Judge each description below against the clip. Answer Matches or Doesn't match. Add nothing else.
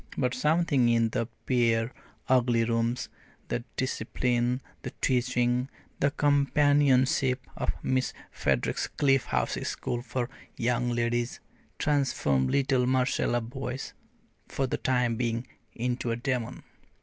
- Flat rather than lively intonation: Matches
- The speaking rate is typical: Doesn't match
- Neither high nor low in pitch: Doesn't match